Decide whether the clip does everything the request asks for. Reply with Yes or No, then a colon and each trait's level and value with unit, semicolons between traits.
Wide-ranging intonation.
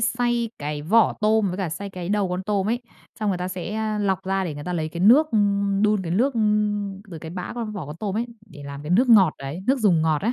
No: average, 4.3 semitones